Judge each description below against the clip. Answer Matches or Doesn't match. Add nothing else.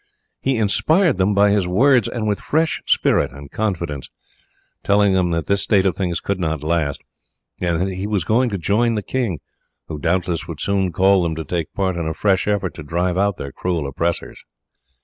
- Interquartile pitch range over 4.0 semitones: Doesn't match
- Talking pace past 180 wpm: Matches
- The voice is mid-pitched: Doesn't match